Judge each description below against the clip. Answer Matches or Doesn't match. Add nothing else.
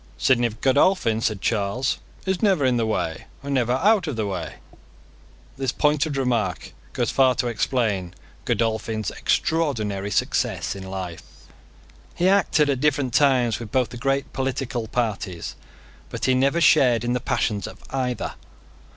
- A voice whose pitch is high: Doesn't match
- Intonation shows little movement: Doesn't match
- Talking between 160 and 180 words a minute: Doesn't match